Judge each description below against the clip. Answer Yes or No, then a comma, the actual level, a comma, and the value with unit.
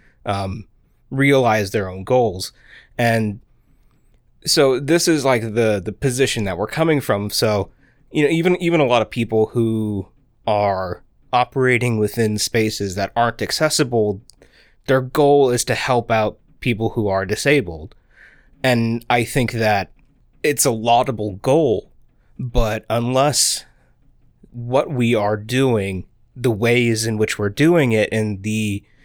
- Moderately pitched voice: No, low, 115 Hz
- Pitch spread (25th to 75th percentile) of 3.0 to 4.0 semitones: Yes, average, 3.7 semitones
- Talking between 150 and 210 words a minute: No, average, 140 wpm